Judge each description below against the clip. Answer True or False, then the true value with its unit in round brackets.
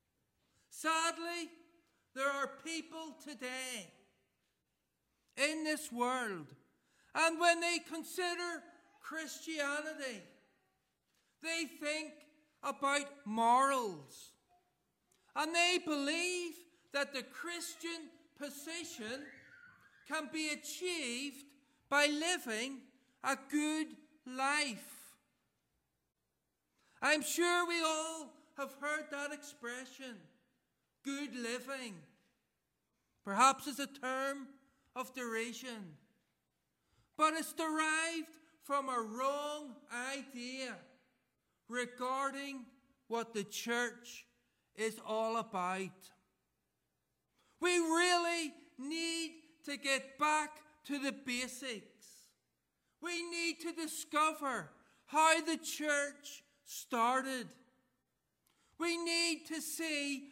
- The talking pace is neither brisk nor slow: False (85 wpm)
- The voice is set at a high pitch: True (285 Hz)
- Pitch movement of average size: True (4.0 semitones)